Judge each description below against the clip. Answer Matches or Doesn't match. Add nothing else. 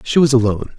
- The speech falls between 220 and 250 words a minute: Matches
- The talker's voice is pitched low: Matches